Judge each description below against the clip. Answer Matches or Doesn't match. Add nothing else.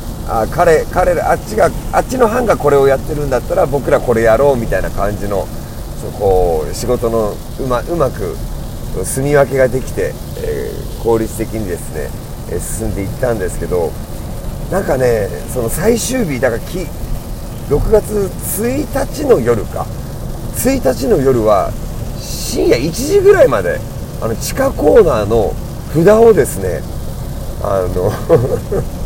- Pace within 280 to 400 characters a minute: Doesn't match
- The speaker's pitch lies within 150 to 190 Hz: Doesn't match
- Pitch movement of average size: Matches